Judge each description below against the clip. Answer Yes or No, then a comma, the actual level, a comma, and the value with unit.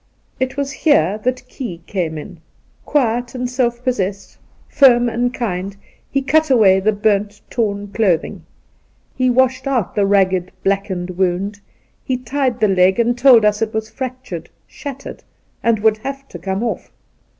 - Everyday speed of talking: Yes, average, 165 wpm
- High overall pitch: Yes, high, 220 Hz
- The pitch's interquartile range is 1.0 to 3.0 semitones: No, average, 4.5 semitones